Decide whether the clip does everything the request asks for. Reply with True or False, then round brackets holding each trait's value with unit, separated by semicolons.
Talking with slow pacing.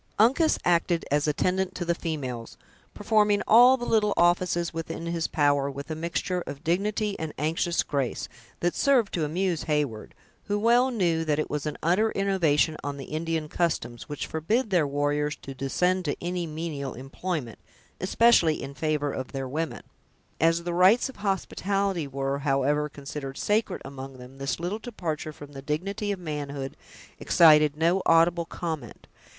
False (165 wpm)